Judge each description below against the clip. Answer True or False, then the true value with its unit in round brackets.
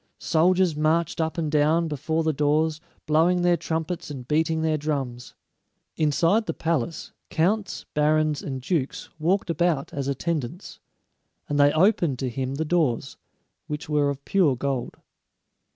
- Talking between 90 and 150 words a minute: True (145 wpm)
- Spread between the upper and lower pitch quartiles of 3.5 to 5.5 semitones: False (2.8 semitones)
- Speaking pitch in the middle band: True (155 Hz)